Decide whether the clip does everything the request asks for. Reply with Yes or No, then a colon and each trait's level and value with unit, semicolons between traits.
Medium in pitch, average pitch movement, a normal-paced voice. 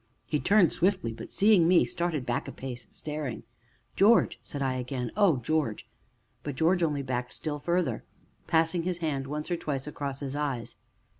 Yes: medium, 150 Hz; average, 4.4 semitones; average, 170 wpm